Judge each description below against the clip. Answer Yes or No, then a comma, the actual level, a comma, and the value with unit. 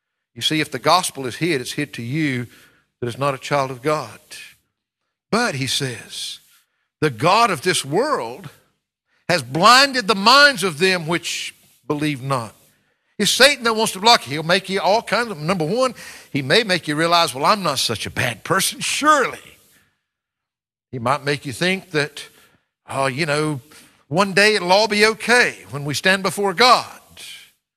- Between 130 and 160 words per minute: No, average, 180 wpm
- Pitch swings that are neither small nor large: No, wide, 6.3 semitones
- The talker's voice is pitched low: No, medium, 170 Hz